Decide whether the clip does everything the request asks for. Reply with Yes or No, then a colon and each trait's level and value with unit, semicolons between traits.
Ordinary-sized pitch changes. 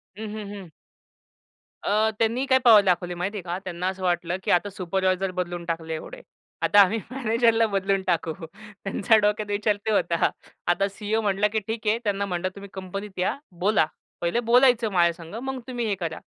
Yes: average, 3.4 semitones